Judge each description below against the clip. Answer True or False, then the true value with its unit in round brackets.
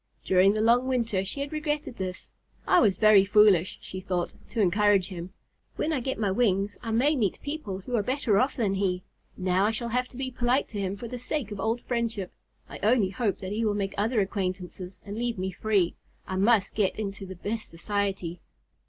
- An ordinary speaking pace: False (215 wpm)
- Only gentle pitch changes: False (3.8 semitones)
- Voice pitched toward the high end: True (205 Hz)